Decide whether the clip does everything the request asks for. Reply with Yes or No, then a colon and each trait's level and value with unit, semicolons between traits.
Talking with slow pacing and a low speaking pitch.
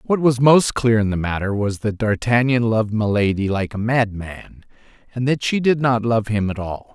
No: fast, 205 wpm; low, 115 Hz